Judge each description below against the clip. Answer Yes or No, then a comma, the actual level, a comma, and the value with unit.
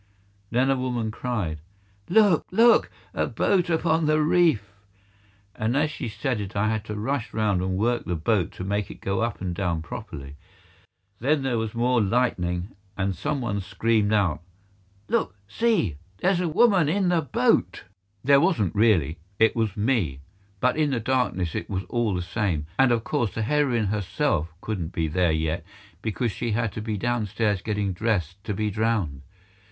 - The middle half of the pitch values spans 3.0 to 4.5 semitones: No, wide, 5.4 semitones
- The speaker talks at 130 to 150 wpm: No, average, 175 wpm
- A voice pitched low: Yes, low, 110 Hz